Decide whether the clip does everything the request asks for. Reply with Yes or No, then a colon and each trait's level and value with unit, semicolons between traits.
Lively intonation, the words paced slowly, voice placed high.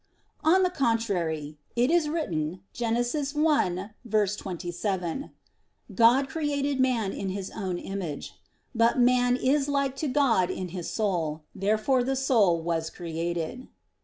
Yes: wide, 7.0 semitones; slow, 125 wpm; high, 225 Hz